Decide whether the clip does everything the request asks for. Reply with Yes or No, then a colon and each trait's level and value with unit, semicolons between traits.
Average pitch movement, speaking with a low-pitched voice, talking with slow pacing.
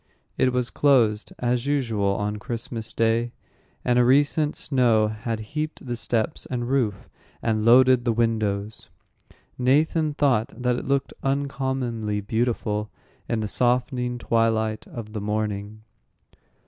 Yes: average, 3.0 semitones; low, 120 Hz; slow, 130 wpm